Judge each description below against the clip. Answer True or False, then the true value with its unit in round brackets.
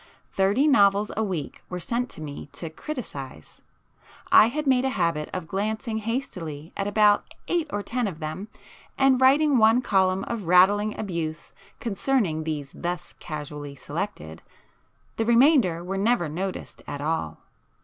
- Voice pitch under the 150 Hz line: False (195 Hz)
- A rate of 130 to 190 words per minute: True (140 wpm)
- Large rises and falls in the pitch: True (6.5 semitones)